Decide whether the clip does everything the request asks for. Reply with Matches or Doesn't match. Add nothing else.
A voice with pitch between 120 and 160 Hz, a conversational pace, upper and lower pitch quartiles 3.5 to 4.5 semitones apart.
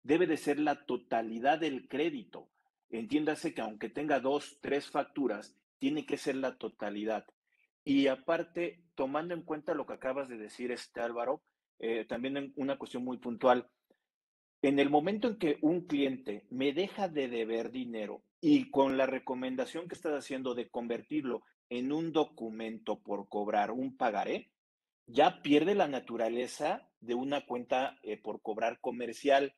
Matches